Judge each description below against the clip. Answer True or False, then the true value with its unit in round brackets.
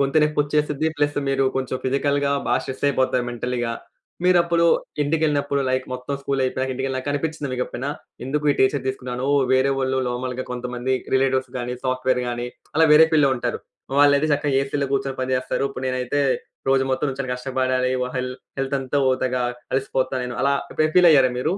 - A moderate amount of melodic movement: False (1.9 semitones)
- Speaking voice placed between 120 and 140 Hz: True (135 Hz)